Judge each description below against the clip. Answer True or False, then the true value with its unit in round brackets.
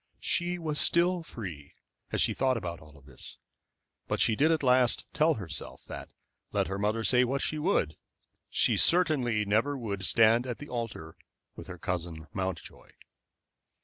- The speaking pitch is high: False (115 Hz)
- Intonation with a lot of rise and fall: True (8.2 semitones)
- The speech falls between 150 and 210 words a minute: True (160 wpm)